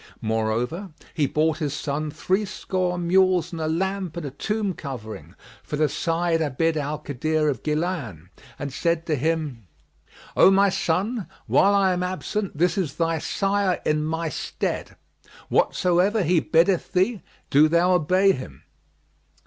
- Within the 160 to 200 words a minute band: No, average, 150 wpm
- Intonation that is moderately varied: Yes, average, 3.7 semitones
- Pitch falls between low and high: Yes, medium, 165 Hz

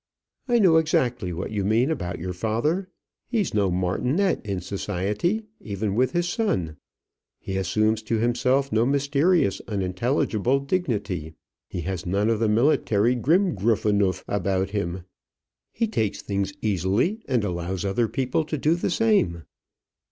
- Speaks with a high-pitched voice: No, low, 110 Hz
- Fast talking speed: No, average, 145 wpm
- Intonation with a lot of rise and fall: Yes, wide, 6.8 semitones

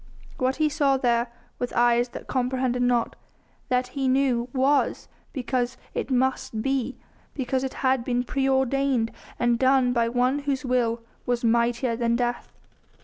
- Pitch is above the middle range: Yes, very high, 250 Hz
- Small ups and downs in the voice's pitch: Yes, narrow, 1.8 semitones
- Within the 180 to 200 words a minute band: No, average, 145 wpm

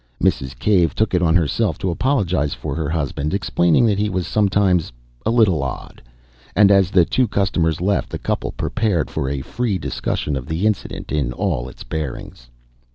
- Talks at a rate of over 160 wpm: Yes, average, 180 wpm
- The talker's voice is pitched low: Yes, very low, 90 Hz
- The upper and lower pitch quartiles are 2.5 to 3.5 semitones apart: No, average, 5.2 semitones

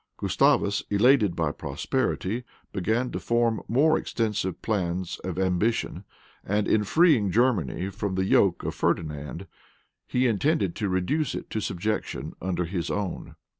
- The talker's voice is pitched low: Yes, low, 100 Hz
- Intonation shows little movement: No, average, 4.2 semitones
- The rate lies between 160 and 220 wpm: No, slow, 135 wpm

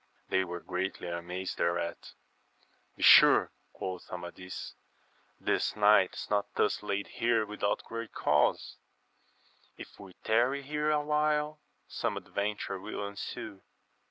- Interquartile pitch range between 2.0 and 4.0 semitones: No, average, 4.5 semitones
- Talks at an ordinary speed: No, slow, 115 wpm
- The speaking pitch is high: No, low, 100 Hz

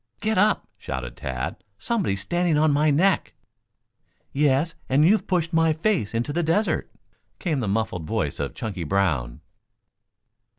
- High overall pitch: No, medium, 150 Hz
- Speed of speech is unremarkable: Yes, average, 145 wpm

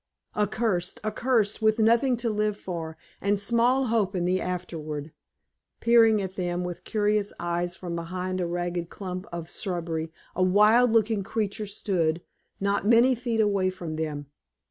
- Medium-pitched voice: No, high, 195 Hz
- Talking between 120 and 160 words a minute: Yes, average, 150 wpm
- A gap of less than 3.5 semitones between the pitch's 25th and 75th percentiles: No, average, 3.9 semitones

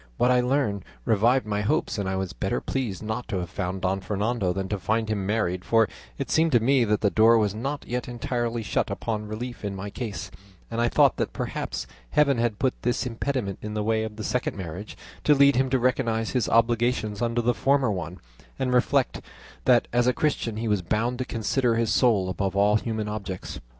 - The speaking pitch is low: Yes, low, 115 Hz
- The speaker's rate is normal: No, fast, 215 wpm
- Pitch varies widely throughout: No, average, 3.2 semitones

